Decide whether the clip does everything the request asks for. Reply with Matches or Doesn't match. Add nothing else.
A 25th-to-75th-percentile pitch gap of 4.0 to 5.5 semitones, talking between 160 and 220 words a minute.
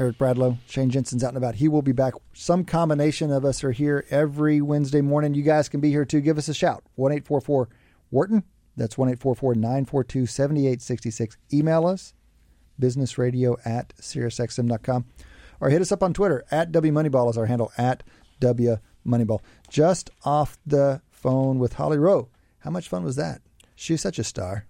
Doesn't match